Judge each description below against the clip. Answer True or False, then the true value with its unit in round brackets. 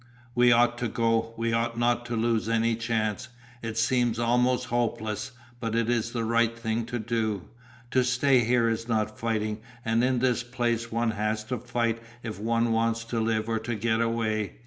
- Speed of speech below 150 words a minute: False (190 wpm)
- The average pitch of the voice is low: True (115 Hz)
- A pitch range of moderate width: False (1.1 semitones)